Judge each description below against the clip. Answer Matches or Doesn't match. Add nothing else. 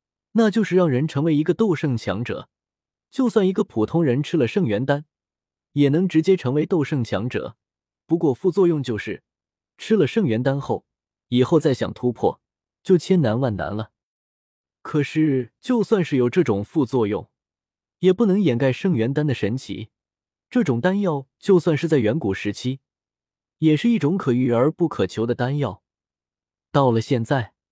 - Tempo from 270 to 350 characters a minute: Doesn't match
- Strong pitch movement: Matches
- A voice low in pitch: Doesn't match